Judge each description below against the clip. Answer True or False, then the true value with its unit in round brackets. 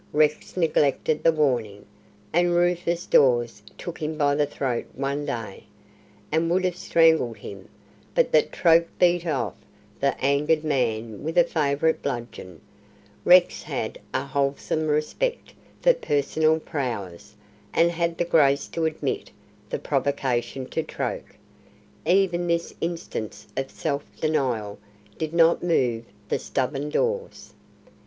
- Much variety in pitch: False (4.2 semitones)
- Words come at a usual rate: False (130 wpm)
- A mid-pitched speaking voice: True (150 Hz)